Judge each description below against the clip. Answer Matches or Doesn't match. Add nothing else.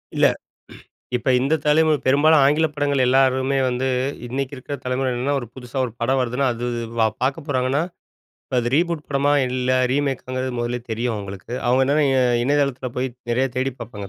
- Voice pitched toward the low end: Matches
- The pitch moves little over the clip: Matches